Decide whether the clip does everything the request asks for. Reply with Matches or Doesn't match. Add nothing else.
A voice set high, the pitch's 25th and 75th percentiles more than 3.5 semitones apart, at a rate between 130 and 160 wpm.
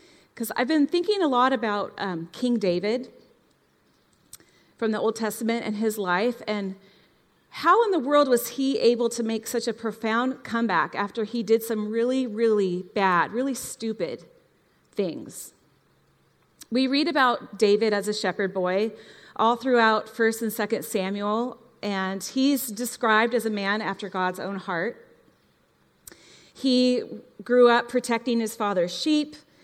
Doesn't match